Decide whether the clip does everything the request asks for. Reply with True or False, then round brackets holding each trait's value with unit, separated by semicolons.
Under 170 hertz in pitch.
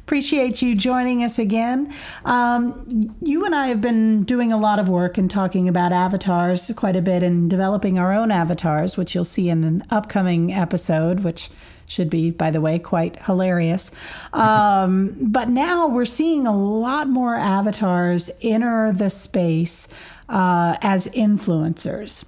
False (200 Hz)